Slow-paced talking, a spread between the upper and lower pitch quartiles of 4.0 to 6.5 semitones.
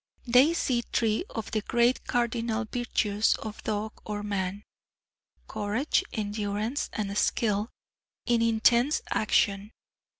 No: slow, 110 wpm; narrow, 2.5 semitones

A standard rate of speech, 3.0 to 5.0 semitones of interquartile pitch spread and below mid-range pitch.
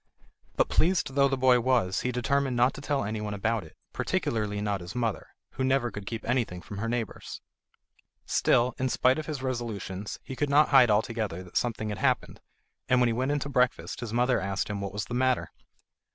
No: fast, 210 wpm; average, 3.9 semitones; low, 120 Hz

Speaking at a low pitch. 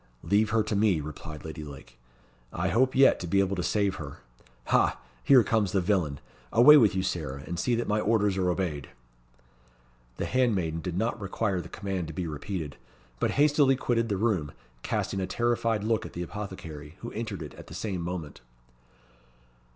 Yes: very low, 95 Hz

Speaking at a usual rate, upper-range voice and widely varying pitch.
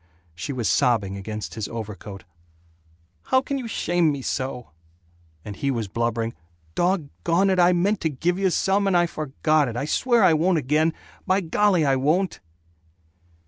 No: average, 170 wpm; medium, 155 Hz; wide, 7.6 semitones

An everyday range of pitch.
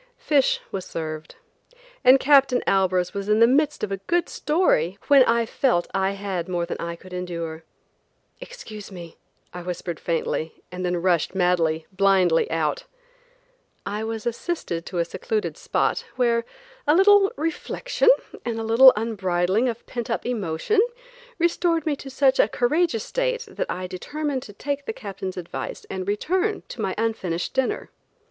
No: wide, 7.5 semitones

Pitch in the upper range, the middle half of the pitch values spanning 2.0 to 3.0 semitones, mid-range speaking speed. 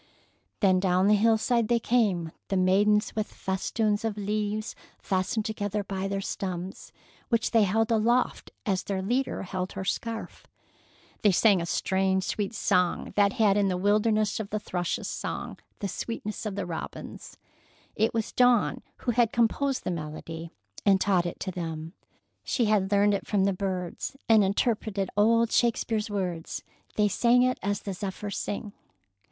Yes: high, 205 Hz; narrow, 2.6 semitones; average, 165 wpm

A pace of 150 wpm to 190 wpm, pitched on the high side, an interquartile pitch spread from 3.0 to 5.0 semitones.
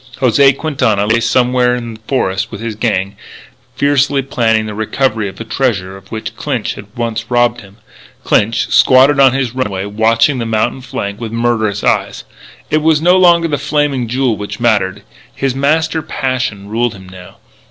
No: average, 175 wpm; low, 120 Hz; average, 4.1 semitones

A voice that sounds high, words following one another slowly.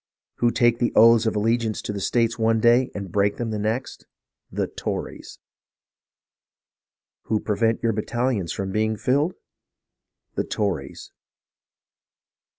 No: low, 115 Hz; slow, 130 wpm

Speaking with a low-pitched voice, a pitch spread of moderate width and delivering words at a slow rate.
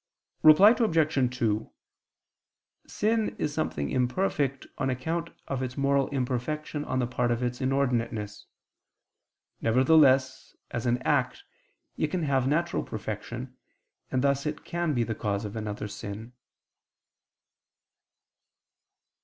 Yes: low, 130 Hz; average, 4.0 semitones; slow, 120 wpm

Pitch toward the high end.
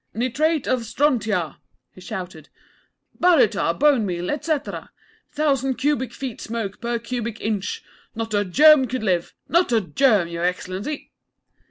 Yes: high, 230 Hz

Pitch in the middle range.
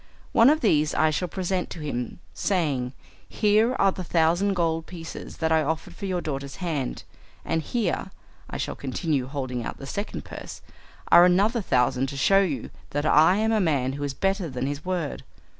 Yes: medium, 160 Hz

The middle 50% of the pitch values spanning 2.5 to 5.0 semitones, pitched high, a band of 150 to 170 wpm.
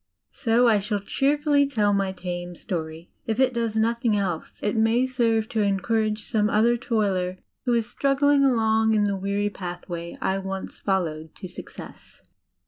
Yes: average, 3.5 semitones; high, 215 Hz; average, 160 wpm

